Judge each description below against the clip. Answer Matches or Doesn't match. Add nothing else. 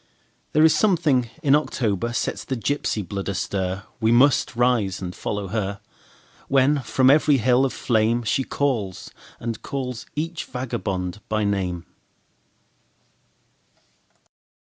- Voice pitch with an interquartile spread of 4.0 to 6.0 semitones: Matches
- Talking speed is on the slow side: Matches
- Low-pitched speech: Matches